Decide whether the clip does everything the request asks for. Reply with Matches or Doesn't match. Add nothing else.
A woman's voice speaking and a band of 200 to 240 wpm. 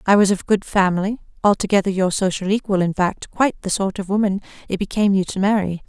Matches